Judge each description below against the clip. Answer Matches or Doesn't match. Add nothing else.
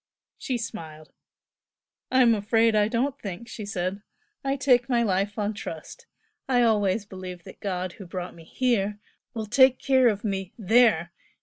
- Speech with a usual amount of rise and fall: Matches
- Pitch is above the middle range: Matches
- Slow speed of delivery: Doesn't match